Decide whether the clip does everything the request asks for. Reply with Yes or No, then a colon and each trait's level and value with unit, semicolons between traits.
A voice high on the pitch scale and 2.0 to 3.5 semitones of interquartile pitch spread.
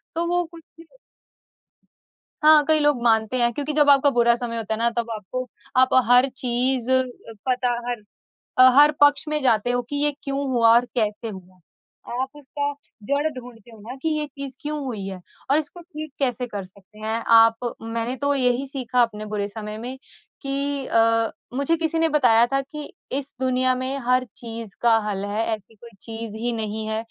No: high, 245 Hz; average, 3.9 semitones